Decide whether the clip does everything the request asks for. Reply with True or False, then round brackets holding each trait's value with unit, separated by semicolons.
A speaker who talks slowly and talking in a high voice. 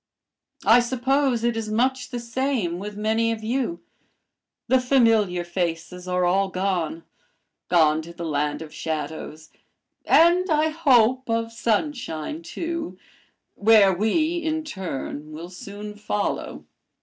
True (125 wpm; 220 Hz)